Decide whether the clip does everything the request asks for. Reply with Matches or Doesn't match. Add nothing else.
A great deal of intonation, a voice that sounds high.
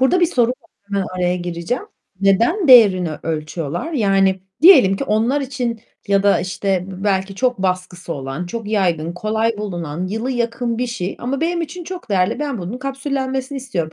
Matches